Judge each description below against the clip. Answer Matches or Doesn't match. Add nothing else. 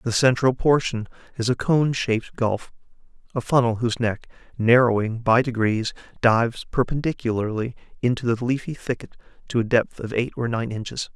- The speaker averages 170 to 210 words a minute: Doesn't match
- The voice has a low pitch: Matches